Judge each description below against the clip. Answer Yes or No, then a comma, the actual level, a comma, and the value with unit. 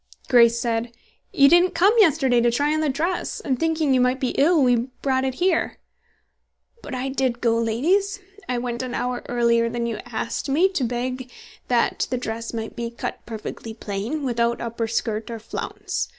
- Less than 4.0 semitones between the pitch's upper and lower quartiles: Yes, average, 3.1 semitones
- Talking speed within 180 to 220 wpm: Yes, average, 185 wpm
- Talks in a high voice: Yes, high, 245 Hz